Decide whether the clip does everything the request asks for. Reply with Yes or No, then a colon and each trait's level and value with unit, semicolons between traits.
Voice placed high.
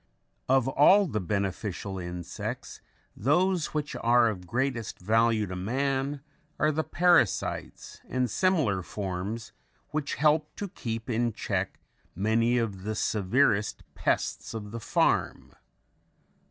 No: low, 115 Hz